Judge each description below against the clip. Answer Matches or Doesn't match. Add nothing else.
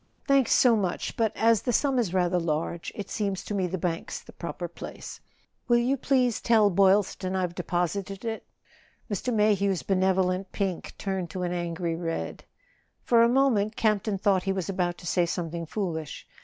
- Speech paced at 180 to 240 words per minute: Matches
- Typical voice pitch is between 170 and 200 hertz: Matches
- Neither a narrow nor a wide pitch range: Matches